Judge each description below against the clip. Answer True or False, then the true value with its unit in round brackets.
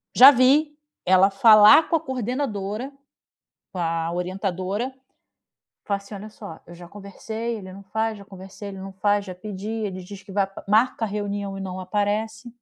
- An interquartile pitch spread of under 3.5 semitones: True (2.6 semitones)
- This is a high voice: True (205 Hz)